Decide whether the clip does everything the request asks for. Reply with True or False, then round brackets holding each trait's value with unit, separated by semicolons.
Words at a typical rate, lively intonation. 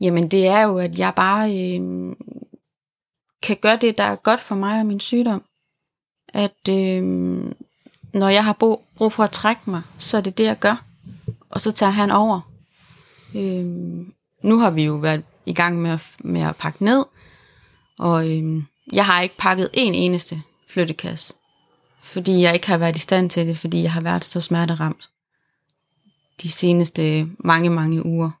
False (175 wpm; 3.8 semitones)